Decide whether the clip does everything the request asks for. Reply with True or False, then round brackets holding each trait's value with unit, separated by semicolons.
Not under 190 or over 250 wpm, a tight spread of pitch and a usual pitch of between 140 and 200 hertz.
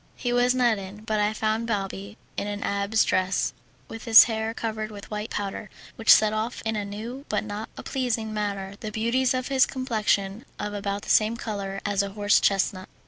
False (200 wpm; 2.0 semitones; 215 Hz)